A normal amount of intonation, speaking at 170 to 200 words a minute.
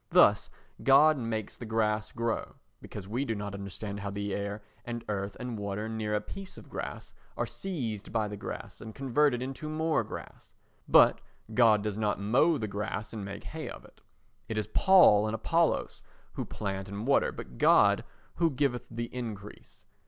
Yes: average, 3.6 semitones; average, 180 wpm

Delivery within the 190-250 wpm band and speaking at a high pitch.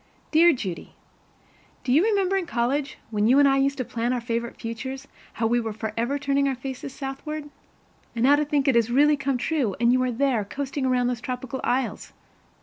Yes: fast, 205 wpm; very high, 260 Hz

